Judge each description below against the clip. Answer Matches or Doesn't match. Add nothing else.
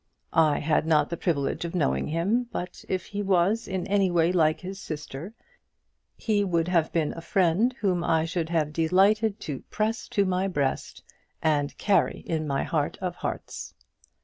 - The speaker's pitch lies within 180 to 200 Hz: Doesn't match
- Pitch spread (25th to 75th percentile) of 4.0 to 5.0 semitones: Doesn't match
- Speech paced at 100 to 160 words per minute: Doesn't match